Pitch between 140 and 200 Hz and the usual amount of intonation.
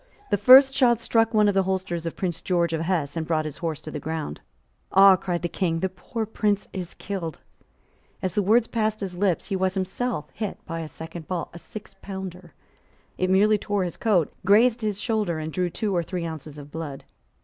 Yes: medium, 185 Hz; average, 3.9 semitones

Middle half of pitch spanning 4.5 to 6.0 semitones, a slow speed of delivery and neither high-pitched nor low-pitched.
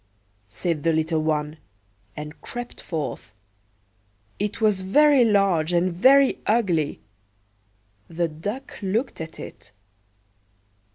Yes: wide, 5.5 semitones; slow, 115 wpm; medium, 175 Hz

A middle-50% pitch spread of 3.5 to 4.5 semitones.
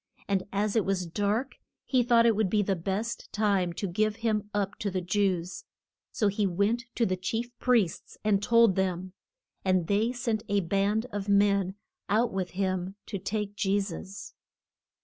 No: narrow, 2.4 semitones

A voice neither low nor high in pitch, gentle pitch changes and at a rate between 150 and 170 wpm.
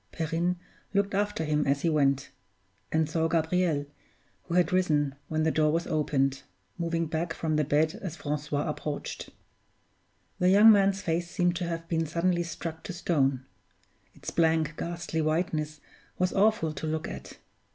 Yes: medium, 160 Hz; narrow, 2.3 semitones; average, 160 wpm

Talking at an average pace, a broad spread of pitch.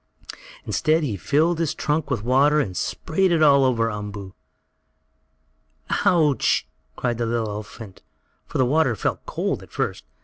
Yes: average, 150 wpm; wide, 5.8 semitones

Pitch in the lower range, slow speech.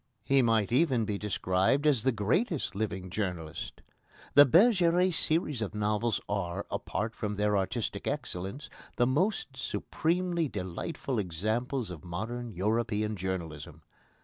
Yes: low, 110 Hz; slow, 125 wpm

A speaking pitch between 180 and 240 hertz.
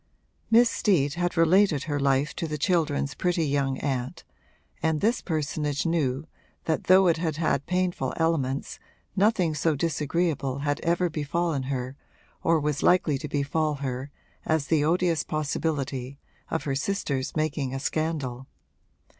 No: medium, 155 Hz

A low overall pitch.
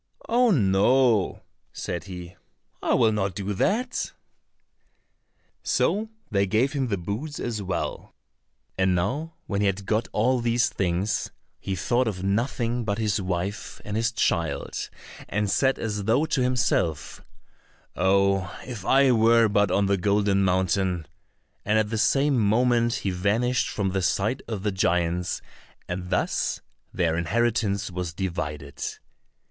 Yes: low, 105 Hz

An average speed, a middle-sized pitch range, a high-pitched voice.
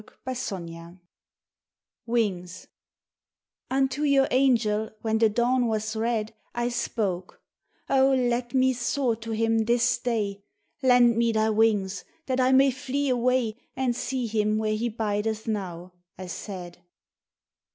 No: slow, 130 wpm; average, 3.0 semitones; high, 230 Hz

